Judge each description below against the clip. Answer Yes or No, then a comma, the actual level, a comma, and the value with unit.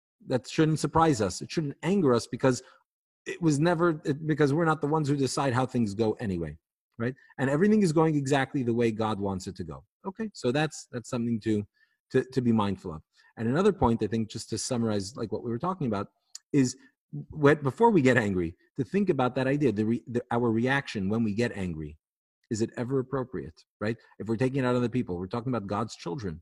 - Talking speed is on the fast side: Yes, fast, 225 wpm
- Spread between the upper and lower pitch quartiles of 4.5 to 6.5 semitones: Yes, average, 4.8 semitones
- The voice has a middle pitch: No, low, 125 Hz